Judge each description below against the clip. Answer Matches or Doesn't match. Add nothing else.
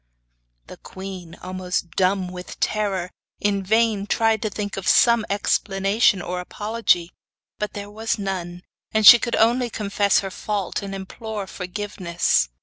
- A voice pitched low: Doesn't match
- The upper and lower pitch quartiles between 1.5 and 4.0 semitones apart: Matches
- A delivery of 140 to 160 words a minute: Matches